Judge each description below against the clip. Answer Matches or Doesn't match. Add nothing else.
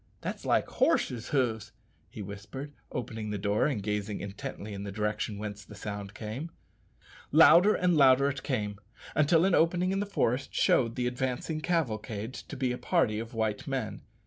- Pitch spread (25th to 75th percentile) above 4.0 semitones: Matches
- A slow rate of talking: Doesn't match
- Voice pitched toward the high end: Doesn't match